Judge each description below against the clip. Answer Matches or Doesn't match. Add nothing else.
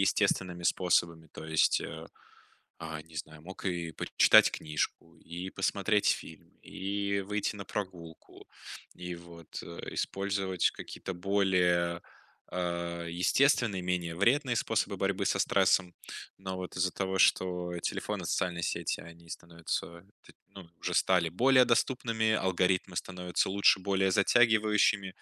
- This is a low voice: Matches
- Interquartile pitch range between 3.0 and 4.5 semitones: Doesn't match